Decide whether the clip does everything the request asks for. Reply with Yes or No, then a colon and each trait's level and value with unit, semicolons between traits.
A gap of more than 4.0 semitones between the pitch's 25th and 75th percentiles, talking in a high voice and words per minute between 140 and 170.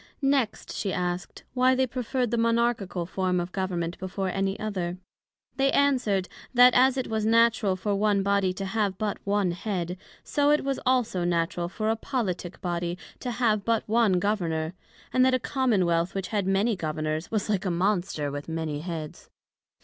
No: average, 4.6 semitones; high, 195 Hz; average, 180 wpm